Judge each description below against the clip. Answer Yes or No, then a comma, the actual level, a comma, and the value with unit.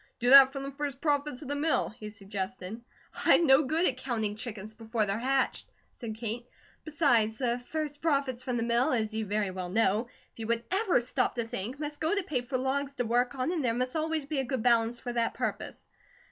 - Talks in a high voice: Yes, high, 245 Hz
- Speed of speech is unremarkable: No, fast, 225 wpm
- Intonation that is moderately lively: Yes, average, 3.9 semitones